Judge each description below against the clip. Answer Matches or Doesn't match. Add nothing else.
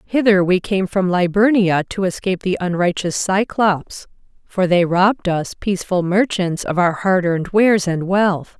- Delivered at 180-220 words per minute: Doesn't match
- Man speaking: Doesn't match